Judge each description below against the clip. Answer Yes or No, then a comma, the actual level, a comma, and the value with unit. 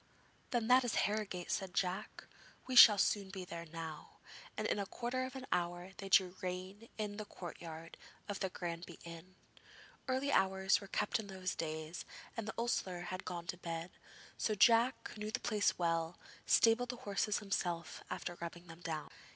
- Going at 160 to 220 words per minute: Yes, average, 180 wpm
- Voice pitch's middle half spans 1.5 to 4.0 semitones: Yes, average, 3.7 semitones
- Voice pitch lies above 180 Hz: Yes, high, 190 Hz